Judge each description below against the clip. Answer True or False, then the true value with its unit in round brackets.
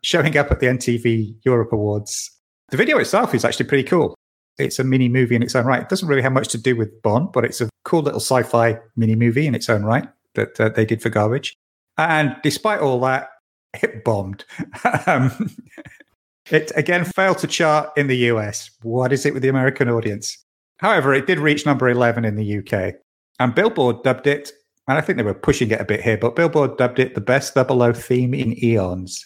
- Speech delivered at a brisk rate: True (215 wpm)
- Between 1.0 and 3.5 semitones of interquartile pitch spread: False (3.9 semitones)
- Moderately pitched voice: False (125 Hz)